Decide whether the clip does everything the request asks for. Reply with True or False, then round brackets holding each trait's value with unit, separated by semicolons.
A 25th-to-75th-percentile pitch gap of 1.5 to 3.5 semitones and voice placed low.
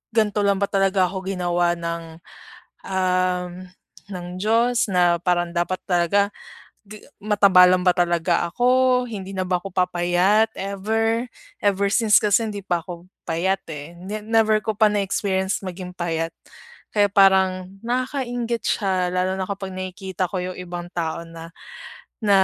False (2.7 semitones; 190 Hz)